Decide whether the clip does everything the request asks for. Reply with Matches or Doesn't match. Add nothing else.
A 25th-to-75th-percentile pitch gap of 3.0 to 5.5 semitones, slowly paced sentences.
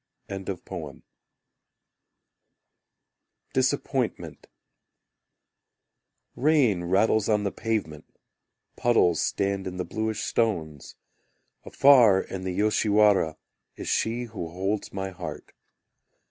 Matches